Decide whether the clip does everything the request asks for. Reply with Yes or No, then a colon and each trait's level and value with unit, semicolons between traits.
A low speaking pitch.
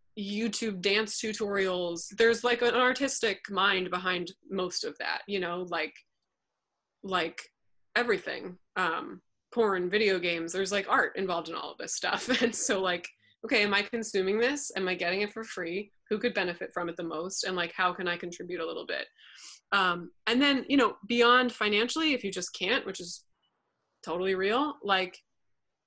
No: high, 195 Hz